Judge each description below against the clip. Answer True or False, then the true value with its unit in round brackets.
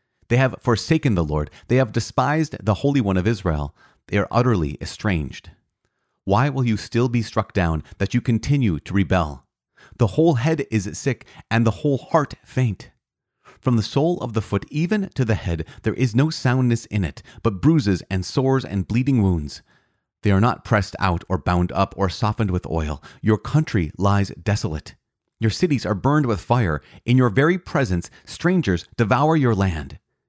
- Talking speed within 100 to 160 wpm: False (180 wpm)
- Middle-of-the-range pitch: False (110 Hz)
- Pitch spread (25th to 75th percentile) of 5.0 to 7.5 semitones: True (5.4 semitones)